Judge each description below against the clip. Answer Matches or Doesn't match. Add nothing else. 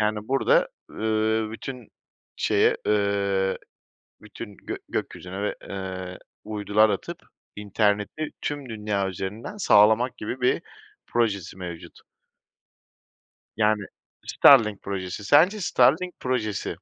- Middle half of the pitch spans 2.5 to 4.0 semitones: Matches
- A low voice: Matches